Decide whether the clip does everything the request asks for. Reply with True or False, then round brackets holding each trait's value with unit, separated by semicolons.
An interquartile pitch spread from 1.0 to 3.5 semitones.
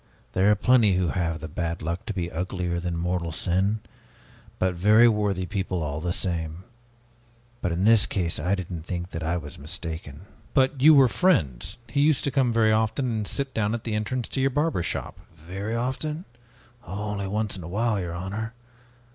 False (4.8 semitones)